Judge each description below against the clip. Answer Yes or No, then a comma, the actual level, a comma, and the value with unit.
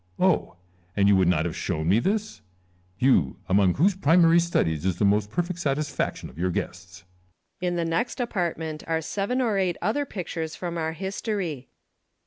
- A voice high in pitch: No, medium, 160 Hz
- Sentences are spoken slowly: No, average, 180 wpm